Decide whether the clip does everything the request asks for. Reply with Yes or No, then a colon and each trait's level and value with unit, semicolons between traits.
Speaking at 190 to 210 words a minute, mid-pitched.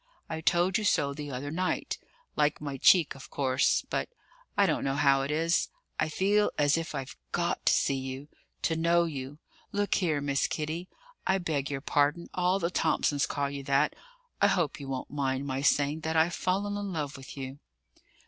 Yes: average, 195 wpm; medium, 150 Hz